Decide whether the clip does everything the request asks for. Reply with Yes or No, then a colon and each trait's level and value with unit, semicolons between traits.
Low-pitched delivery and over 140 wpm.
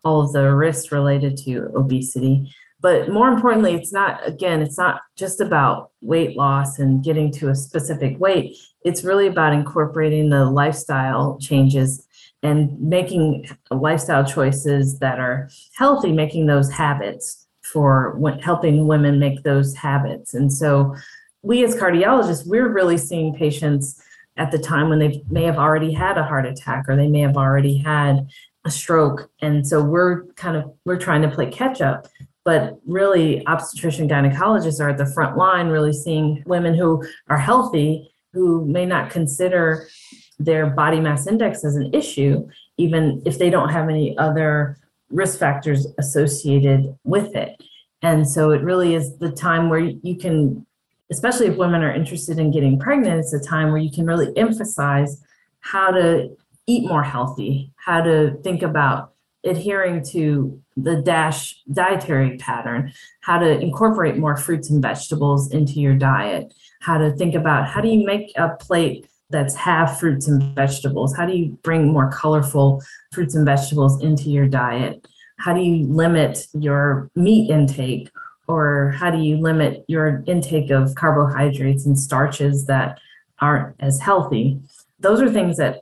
No: medium, 155 Hz; average, 160 wpm